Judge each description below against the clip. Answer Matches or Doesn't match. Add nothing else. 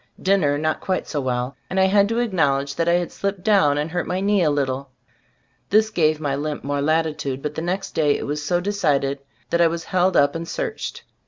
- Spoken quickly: Matches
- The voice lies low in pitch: Doesn't match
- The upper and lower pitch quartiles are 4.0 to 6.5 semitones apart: Matches